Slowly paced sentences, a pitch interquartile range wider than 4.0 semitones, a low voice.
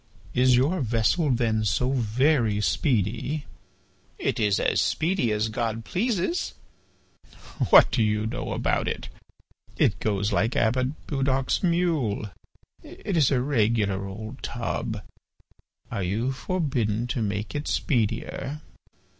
Yes: slow, 120 wpm; average, 4.7 semitones; low, 120 Hz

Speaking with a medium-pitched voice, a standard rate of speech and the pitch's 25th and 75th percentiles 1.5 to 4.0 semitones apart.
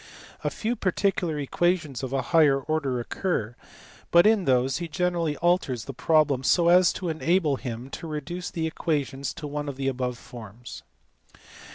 No: medium, 150 Hz; average, 170 wpm; average, 4.6 semitones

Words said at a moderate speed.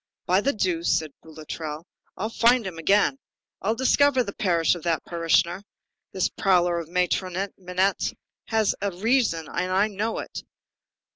Yes: average, 150 wpm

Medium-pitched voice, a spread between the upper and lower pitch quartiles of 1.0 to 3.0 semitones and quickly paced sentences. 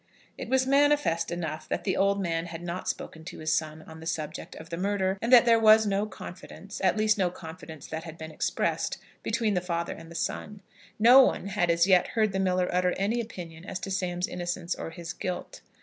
No: medium, 180 Hz; average, 3.7 semitones; fast, 220 wpm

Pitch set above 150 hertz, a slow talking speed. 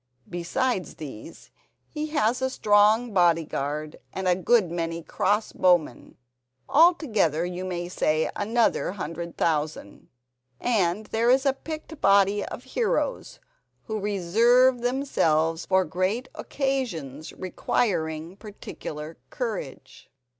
Yes: high, 190 Hz; slow, 110 wpm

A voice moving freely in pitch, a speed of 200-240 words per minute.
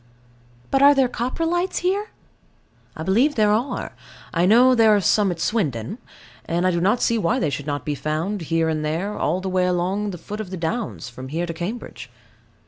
Yes: wide, 5.8 semitones; fast, 205 wpm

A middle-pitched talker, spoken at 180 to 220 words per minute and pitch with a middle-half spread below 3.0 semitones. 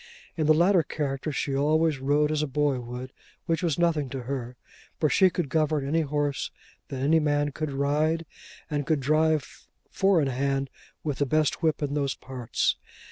Yes: medium, 145 Hz; average, 185 wpm; narrow, 2.4 semitones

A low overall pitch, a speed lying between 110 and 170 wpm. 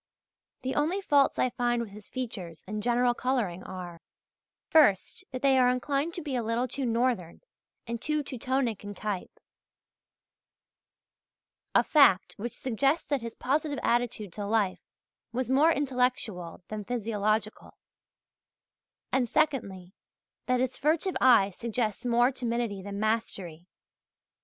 No: high, 240 Hz; slow, 135 wpm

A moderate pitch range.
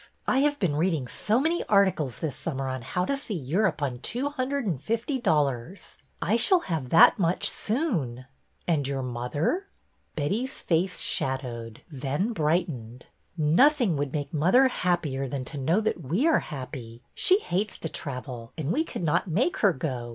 No: wide, 8.4 semitones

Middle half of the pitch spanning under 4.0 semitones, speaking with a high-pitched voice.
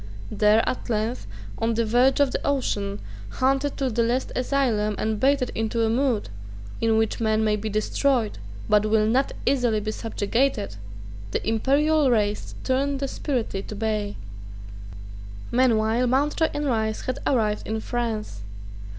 Yes: average, 3.5 semitones; high, 230 Hz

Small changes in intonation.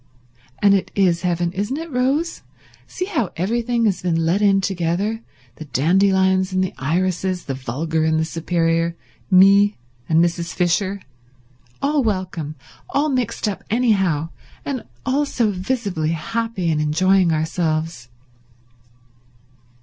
No: average, 4.3 semitones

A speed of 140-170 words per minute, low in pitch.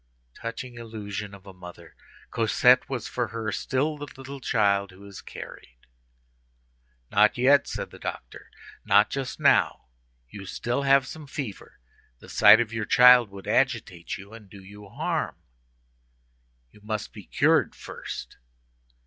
Yes: average, 145 wpm; low, 110 Hz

